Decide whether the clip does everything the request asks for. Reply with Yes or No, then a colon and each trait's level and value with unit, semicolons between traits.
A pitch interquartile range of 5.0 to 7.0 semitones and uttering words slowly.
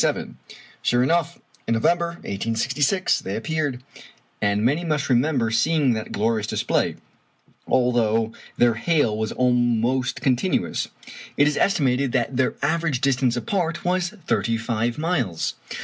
Yes: average, 5.3 semitones; slow, 125 wpm